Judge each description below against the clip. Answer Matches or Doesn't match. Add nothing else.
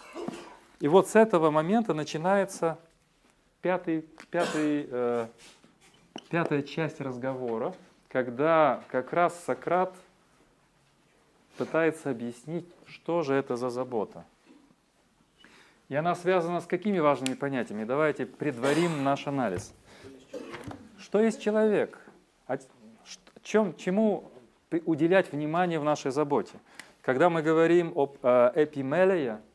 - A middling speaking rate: Doesn't match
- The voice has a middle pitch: Matches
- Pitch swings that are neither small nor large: Matches